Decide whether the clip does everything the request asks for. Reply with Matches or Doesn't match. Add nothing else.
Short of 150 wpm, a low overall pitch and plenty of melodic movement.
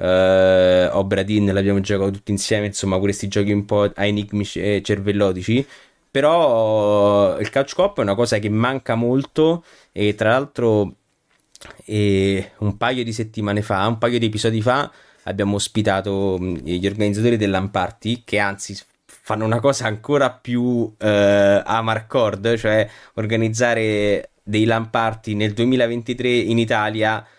Doesn't match